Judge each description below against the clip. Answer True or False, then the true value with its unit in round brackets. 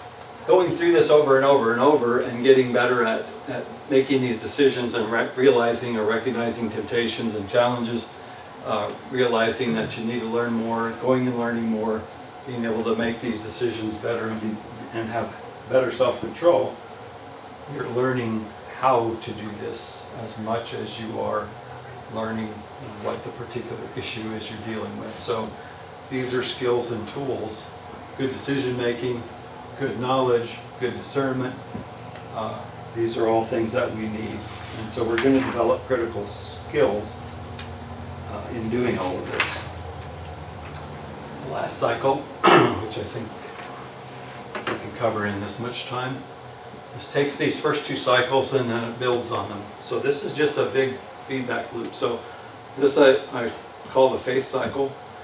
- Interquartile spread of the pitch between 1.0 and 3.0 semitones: True (2.5 semitones)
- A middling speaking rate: True (160 wpm)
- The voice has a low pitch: True (115 Hz)